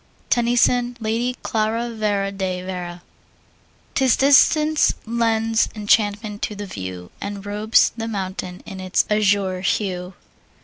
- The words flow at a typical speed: No, slow, 120 wpm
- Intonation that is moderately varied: Yes, average, 3.3 semitones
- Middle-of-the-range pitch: No, high, 210 Hz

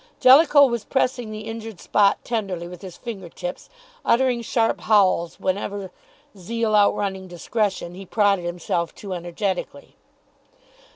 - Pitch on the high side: Yes, high, 200 Hz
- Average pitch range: Yes, average, 4.0 semitones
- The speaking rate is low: Yes, slow, 125 wpm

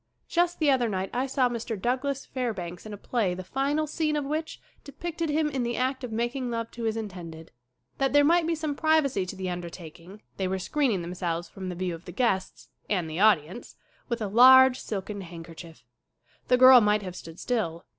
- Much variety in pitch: Yes, wide, 6.6 semitones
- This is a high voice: Yes, high, 230 Hz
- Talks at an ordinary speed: No, fast, 215 wpm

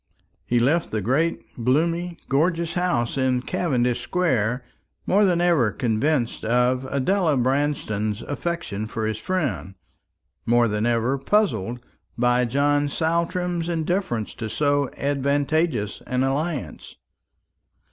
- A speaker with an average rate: No, slow, 115 wpm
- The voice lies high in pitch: No, low, 135 Hz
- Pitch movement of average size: No, wide, 5.9 semitones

